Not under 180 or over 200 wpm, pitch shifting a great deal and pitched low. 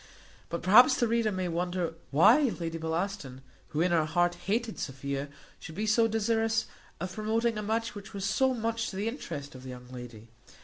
No: average, 190 wpm; wide, 5.7 semitones; high, 190 Hz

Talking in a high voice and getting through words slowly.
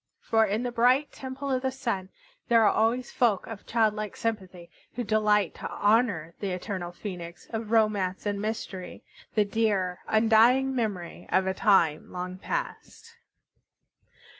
No: high, 215 Hz; average, 145 wpm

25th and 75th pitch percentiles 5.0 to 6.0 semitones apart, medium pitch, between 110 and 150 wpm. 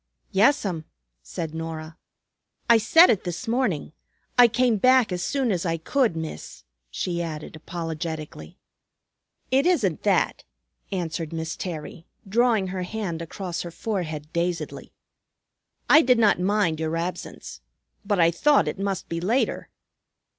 Yes: average, 5.3 semitones; medium, 180 Hz; slow, 135 wpm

